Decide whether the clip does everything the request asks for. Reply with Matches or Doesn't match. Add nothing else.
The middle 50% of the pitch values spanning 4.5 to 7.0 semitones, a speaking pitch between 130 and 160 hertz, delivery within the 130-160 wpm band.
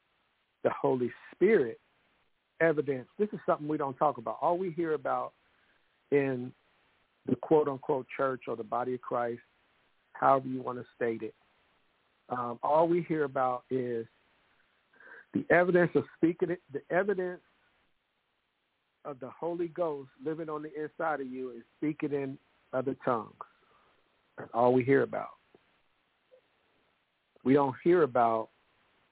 Matches